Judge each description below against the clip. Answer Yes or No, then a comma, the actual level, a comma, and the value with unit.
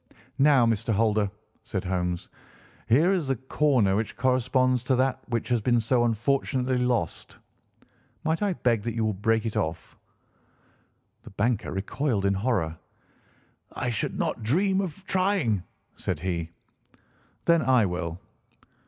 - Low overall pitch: Yes, low, 120 Hz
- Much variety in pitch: No, average, 4.8 semitones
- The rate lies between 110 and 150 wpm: Yes, average, 140 wpm